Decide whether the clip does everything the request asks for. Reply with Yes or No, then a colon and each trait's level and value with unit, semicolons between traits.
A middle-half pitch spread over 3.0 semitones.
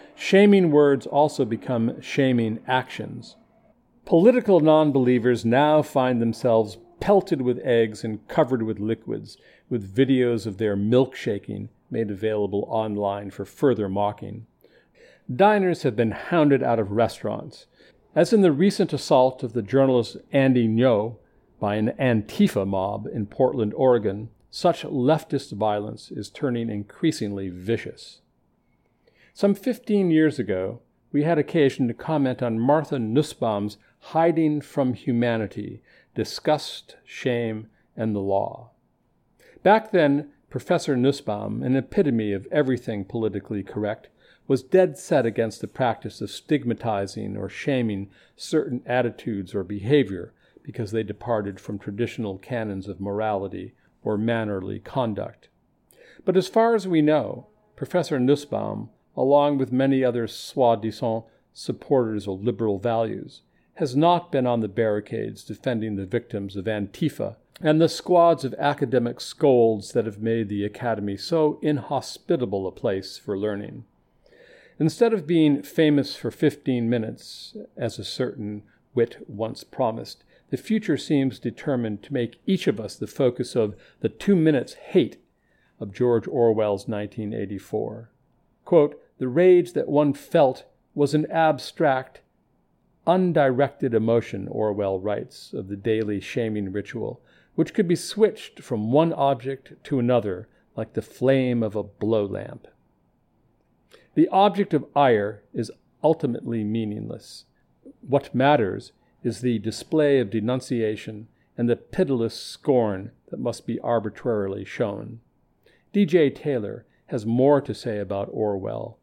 Yes: average, 5.2 semitones